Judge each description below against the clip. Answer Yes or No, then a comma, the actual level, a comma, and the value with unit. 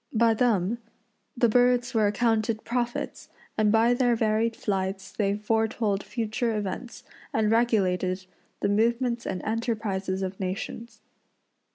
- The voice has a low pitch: No, high, 220 Hz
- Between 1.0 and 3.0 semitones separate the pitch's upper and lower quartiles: Yes, average, 2.7 semitones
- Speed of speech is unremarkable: No, slow, 125 wpm